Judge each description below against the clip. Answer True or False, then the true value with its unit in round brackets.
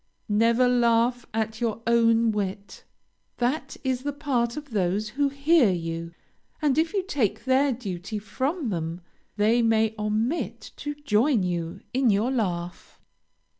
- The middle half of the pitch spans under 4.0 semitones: False (4.3 semitones)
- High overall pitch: True (230 Hz)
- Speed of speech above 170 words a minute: False (140 wpm)